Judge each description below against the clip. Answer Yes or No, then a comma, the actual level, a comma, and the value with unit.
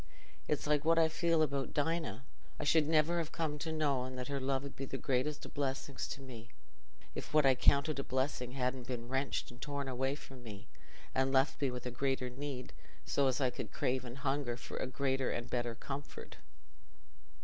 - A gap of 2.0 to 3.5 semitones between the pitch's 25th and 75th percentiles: Yes, narrow, 2.4 semitones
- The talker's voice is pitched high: No, low, 135 Hz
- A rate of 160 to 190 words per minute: No, fast, 205 wpm